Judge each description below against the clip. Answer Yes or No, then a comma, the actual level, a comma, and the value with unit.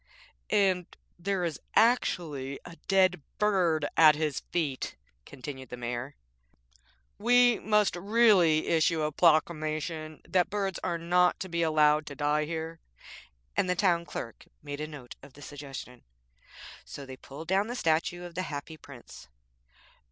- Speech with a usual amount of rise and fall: Yes, average, 3.7 semitones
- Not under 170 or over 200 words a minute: No, average, 145 wpm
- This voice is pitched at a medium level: Yes, medium, 160 Hz